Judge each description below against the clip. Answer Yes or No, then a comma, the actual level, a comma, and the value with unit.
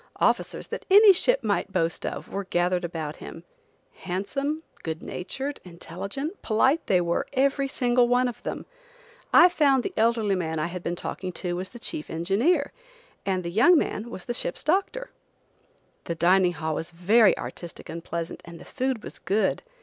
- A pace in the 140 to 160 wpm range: No, average, 175 wpm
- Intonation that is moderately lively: No, wide, 7.5 semitones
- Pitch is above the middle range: Yes, high, 200 Hz